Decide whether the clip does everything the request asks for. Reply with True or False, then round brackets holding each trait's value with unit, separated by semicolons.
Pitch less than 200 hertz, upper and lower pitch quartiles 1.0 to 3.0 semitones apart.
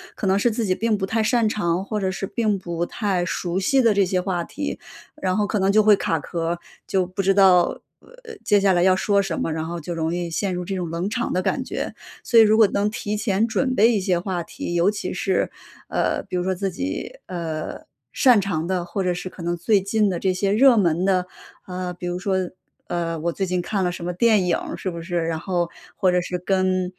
True (185 Hz; 2.7 semitones)